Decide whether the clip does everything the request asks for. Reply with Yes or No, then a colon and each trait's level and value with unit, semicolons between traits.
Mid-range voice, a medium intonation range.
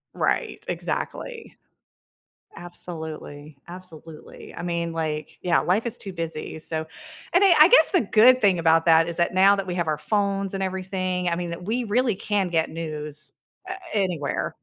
Yes: medium, 175 Hz; average, 3.6 semitones